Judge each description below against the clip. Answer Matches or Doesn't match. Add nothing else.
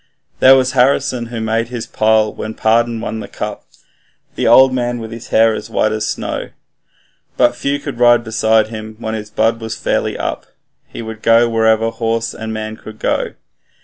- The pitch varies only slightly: Matches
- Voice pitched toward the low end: Matches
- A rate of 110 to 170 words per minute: Doesn't match